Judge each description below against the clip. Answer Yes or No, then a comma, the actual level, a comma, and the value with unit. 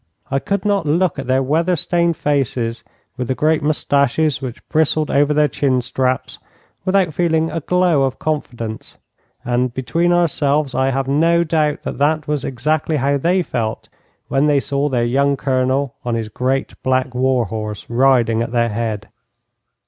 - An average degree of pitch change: Yes, average, 3.7 semitones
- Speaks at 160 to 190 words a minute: Yes, average, 165 wpm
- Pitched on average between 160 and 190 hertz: No, medium, 140 Hz